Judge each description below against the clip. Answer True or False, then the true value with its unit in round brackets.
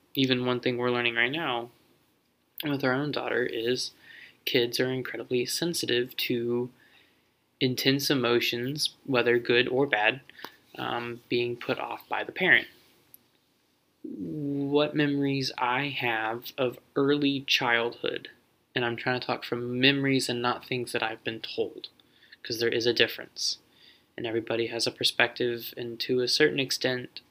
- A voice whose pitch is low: True (125 Hz)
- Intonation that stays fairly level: True (2.2 semitones)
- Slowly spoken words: False (145 wpm)